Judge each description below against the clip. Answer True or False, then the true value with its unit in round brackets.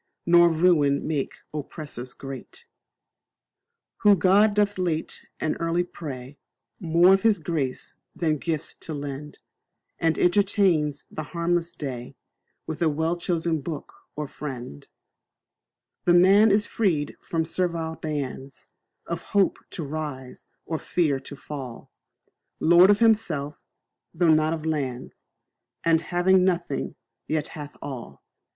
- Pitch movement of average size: True (3.3 semitones)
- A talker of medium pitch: True (160 Hz)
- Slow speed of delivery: True (125 wpm)